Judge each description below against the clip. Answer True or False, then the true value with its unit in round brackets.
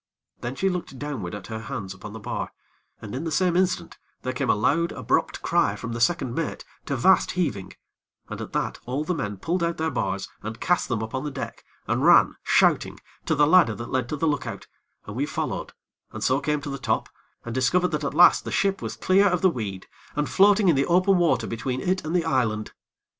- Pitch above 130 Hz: True (140 Hz)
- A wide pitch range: True (7.0 semitones)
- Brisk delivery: True (230 wpm)